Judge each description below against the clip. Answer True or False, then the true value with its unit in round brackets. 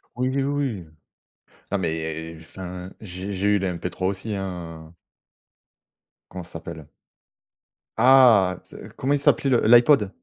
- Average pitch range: False (5.9 semitones)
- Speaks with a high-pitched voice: False (95 Hz)